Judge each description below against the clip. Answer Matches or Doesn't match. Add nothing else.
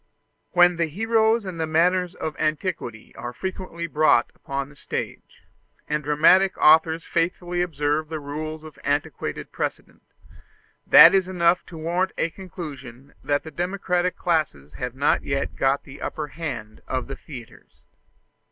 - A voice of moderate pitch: Matches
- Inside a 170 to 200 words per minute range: Doesn't match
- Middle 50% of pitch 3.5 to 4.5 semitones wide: Matches